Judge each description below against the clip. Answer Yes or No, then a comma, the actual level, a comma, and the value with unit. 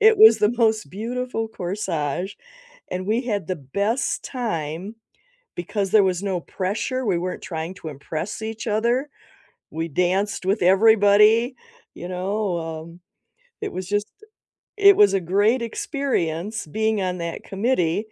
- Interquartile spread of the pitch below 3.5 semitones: No, average, 3.8 semitones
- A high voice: Yes, high, 200 Hz